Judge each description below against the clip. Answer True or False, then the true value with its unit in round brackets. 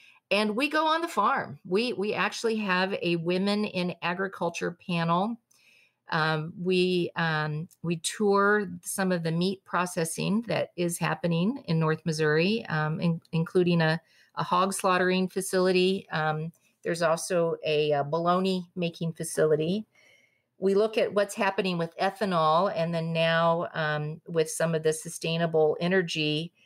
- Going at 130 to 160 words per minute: True (145 wpm)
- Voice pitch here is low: False (175 Hz)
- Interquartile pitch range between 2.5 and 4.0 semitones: True (2.8 semitones)